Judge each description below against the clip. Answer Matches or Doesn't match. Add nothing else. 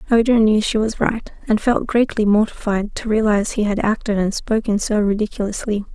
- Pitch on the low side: Doesn't match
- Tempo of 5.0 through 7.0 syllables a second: Matches